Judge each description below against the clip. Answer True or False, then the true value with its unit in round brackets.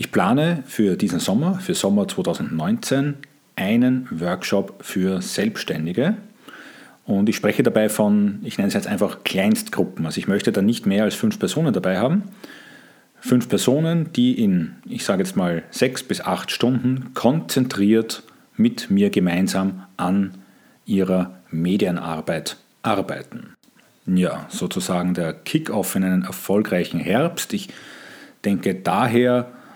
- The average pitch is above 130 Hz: False (125 Hz)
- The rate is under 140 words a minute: True (130 wpm)